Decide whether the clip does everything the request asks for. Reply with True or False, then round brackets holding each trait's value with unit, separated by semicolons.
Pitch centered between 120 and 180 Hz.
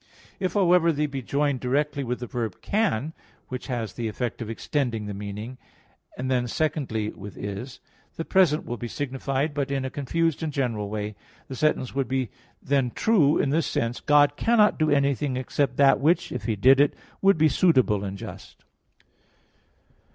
True (135 Hz)